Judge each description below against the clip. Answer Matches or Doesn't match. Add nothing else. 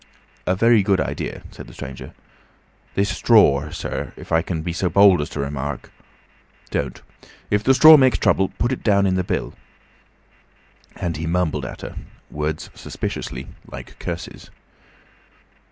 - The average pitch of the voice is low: Matches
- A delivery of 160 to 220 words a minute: Doesn't match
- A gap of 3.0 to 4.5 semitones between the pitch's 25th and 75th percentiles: Doesn't match